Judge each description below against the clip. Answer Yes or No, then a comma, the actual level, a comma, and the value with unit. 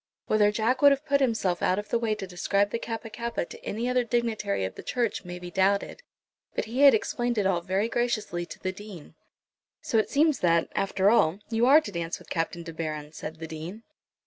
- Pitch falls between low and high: No, high, 205 Hz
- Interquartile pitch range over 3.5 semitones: Yes, average, 5.1 semitones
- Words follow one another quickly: Yes, fast, 225 wpm